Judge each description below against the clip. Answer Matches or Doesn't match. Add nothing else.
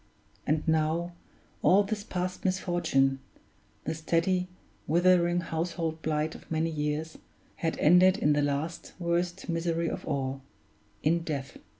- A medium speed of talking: Doesn't match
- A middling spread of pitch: Doesn't match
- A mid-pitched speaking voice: Matches